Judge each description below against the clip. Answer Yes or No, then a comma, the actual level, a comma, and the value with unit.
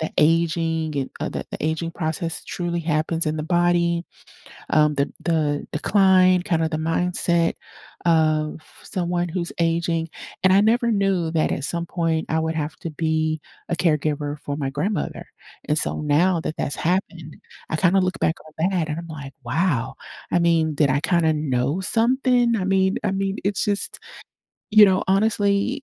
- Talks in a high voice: No, medium, 165 Hz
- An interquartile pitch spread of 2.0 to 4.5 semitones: Yes, average, 3.1 semitones